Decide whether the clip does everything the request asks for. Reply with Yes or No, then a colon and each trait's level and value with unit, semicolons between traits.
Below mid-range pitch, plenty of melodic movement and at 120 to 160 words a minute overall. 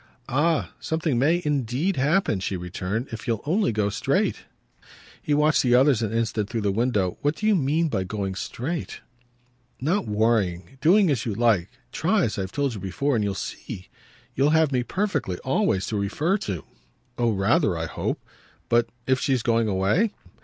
No: low, 120 Hz; wide, 6.4 semitones; average, 175 wpm